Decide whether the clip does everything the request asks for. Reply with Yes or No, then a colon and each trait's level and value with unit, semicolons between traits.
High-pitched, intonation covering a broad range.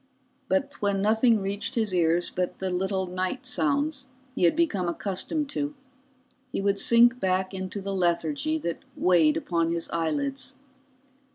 Yes: high, 195 Hz; wide, 6.8 semitones